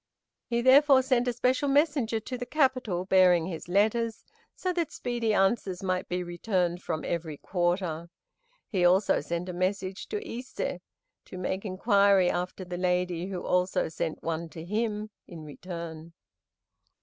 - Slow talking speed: No, average, 150 wpm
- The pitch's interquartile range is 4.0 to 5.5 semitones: Yes, average, 5.0 semitones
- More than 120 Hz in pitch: Yes, medium, 185 Hz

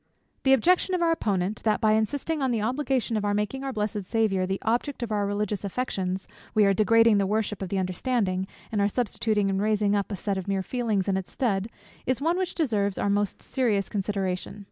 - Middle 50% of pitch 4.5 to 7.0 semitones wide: No, average, 3.5 semitones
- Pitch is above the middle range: Yes, high, 210 Hz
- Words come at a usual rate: No, fast, 215 wpm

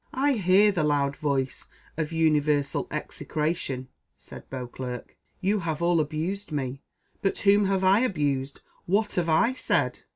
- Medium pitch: Yes, medium, 160 Hz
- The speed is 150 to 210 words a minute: No, average, 140 wpm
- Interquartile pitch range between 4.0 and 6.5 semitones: Yes, wide, 5.5 semitones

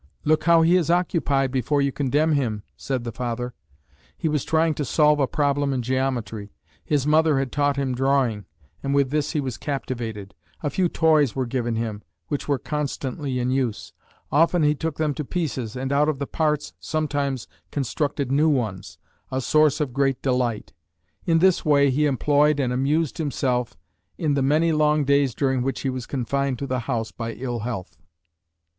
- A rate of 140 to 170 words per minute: No, average, 185 wpm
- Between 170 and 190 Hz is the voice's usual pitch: No, medium, 140 Hz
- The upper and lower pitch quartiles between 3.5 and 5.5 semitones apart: No, average, 3.0 semitones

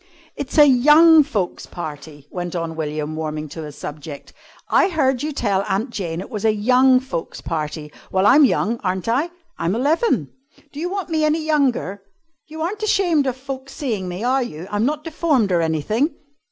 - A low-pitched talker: No, high, 235 Hz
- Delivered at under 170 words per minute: No, average, 185 wpm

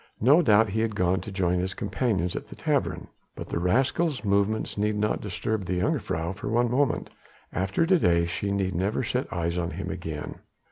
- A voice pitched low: Yes, low, 100 Hz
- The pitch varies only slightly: No, average, 3.8 semitones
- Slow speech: No, average, 195 wpm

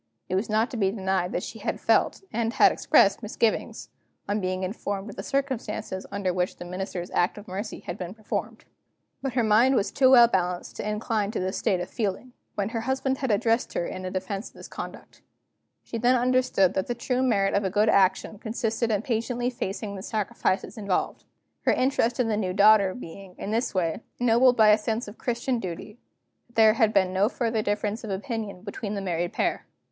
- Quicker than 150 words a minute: Yes, fast, 205 wpm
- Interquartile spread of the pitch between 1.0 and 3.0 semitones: No, average, 3.5 semitones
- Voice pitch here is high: Yes, high, 210 Hz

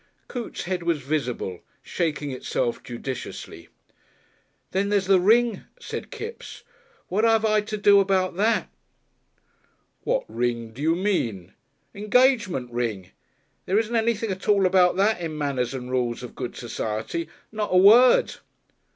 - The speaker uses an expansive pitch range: Yes, wide, 8.9 semitones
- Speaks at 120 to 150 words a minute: Yes, average, 140 wpm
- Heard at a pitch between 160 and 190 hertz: Yes, medium, 185 Hz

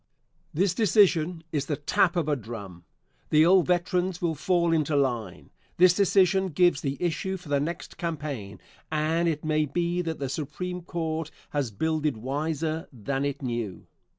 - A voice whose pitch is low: No, medium, 160 Hz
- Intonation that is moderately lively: Yes, average, 3.7 semitones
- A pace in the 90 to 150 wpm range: No, average, 160 wpm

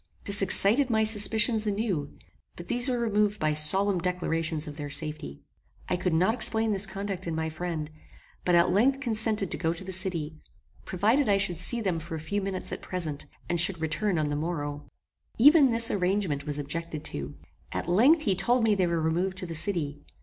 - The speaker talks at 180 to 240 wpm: Yes, average, 200 wpm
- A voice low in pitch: No, medium, 185 Hz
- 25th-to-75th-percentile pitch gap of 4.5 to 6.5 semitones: Yes, average, 4.8 semitones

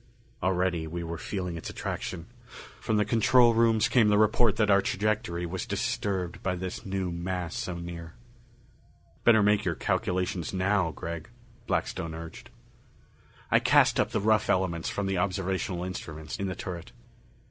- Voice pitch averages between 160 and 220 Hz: No, very low, 95 Hz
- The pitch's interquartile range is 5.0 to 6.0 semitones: No, average, 3.3 semitones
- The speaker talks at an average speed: Yes, average, 155 wpm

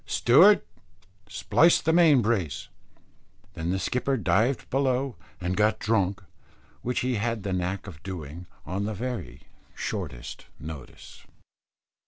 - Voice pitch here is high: No, low, 105 Hz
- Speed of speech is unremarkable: No, slow, 125 wpm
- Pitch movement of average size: No, wide, 5.7 semitones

